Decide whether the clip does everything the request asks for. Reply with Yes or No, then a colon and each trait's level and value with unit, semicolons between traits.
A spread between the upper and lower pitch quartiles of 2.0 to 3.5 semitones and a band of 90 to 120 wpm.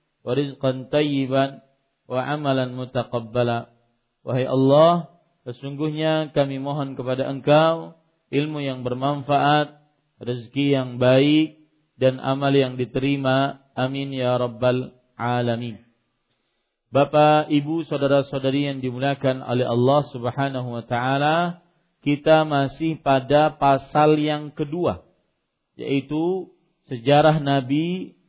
Yes: average, 2.8 semitones; average, 100 wpm